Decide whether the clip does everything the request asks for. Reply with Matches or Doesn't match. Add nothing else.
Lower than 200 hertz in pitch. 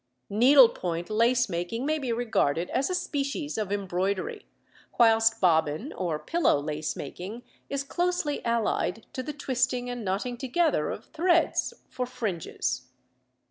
Doesn't match